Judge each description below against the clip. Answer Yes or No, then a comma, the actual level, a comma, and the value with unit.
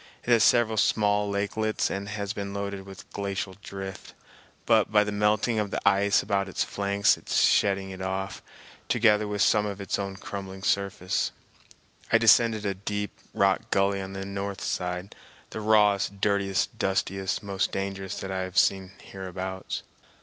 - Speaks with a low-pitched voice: Yes, low, 100 Hz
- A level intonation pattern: Yes, narrow, 1.2 semitones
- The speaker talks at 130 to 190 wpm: Yes, average, 165 wpm